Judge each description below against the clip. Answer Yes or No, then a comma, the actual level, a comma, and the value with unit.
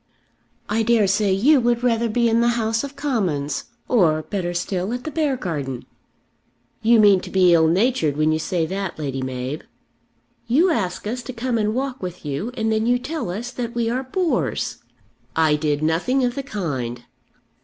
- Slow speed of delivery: No, average, 185 wpm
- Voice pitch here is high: Yes, high, 215 Hz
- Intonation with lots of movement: Yes, wide, 7.1 semitones